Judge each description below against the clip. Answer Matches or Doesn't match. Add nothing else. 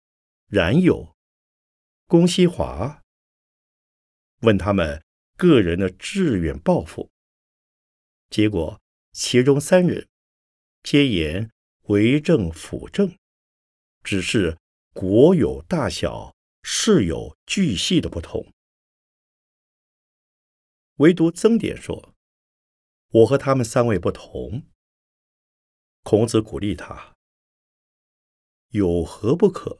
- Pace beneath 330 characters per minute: Matches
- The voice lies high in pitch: Doesn't match